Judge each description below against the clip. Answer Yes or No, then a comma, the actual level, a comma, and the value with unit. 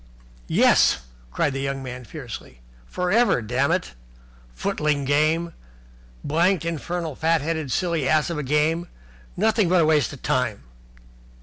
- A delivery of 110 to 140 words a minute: Yes, slow, 135 wpm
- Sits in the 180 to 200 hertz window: No, medium, 155 Hz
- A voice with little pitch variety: No, average, 3.8 semitones